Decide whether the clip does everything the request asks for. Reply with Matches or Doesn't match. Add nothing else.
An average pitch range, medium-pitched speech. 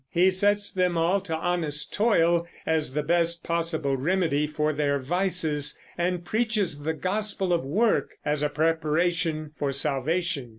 Matches